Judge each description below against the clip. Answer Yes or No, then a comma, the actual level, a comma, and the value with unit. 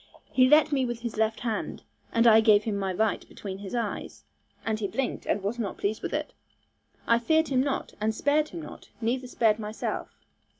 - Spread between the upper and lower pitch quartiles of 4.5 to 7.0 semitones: No, average, 3.1 semitones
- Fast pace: Yes, fast, 210 wpm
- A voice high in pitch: Yes, high, 230 Hz